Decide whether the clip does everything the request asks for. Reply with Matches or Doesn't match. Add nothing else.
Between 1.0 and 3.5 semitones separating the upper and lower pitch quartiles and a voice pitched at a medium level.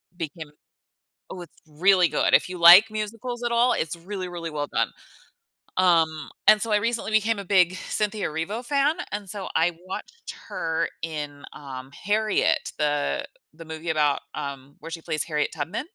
Doesn't match